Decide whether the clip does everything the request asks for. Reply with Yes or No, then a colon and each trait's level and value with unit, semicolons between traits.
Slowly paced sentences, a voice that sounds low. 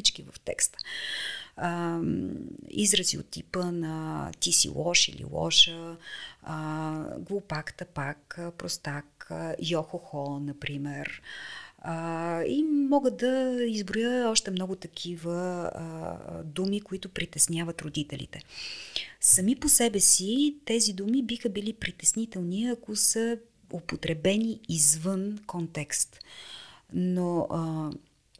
No: slow, 90 wpm; medium, 180 Hz